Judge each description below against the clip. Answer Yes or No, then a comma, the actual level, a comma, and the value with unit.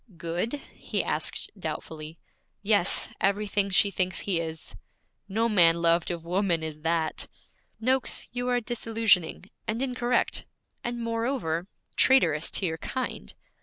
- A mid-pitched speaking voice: No, high, 195 Hz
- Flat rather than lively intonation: No, wide, 5.6 semitones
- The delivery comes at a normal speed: No, slow, 130 wpm